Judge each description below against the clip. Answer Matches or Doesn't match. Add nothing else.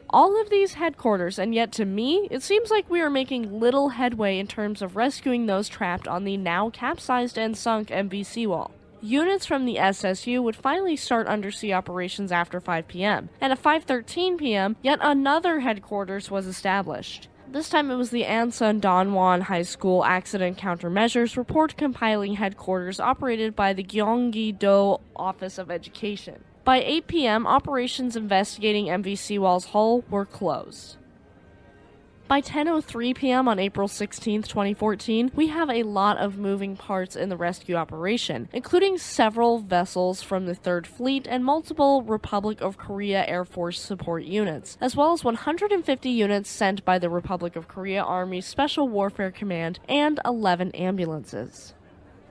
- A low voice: Doesn't match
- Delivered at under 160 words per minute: Matches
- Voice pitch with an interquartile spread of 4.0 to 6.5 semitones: Matches